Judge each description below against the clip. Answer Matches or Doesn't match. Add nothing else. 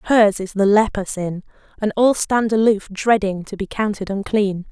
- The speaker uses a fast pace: Doesn't match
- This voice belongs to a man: Doesn't match